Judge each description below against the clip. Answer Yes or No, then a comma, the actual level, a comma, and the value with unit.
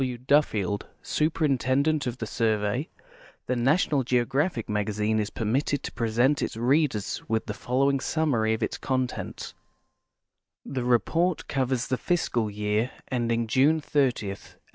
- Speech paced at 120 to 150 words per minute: Yes, slow, 135 wpm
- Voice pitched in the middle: No, low, 125 Hz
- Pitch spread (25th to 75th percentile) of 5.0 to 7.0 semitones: No, average, 4.1 semitones